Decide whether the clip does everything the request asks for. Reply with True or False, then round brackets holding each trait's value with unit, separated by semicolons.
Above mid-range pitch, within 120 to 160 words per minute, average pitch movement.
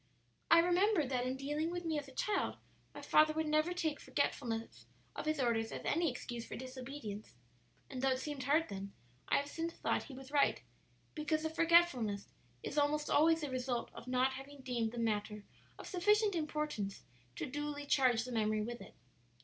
False (280 Hz; 190 wpm; 4.2 semitones)